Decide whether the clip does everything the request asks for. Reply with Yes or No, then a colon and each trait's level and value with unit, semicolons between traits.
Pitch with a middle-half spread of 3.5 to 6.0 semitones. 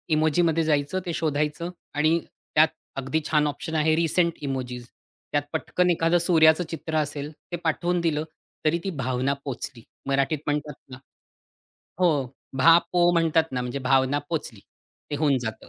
No: average, 3.0 semitones